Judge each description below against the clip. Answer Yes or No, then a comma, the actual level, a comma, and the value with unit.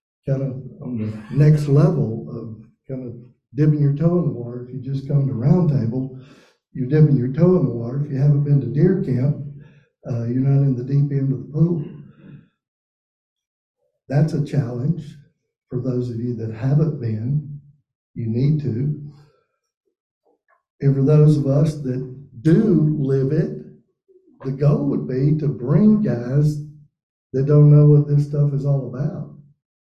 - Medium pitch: Yes, medium, 145 Hz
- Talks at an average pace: Yes, average, 170 wpm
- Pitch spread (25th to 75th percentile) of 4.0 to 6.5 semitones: No, average, 2.7 semitones